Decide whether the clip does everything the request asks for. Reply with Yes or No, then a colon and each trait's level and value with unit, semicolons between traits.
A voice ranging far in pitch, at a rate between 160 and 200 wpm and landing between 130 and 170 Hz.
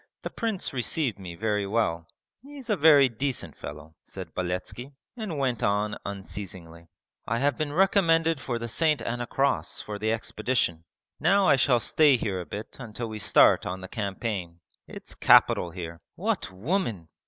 No: wide, 7.3 semitones; average, 165 wpm; low, 115 Hz